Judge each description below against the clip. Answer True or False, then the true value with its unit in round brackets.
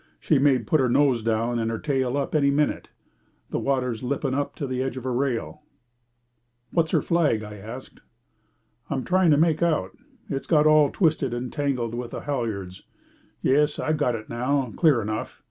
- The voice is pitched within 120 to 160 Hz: True (135 Hz)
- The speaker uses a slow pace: False (185 wpm)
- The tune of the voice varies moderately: True (3.8 semitones)